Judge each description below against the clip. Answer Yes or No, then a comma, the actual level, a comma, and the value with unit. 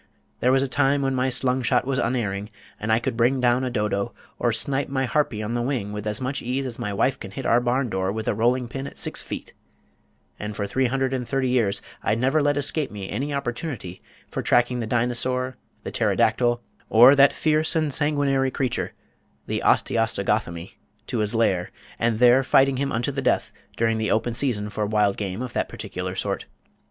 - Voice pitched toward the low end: Yes, low, 120 Hz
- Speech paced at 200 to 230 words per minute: Yes, fast, 205 wpm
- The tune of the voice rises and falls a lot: No, average, 3.6 semitones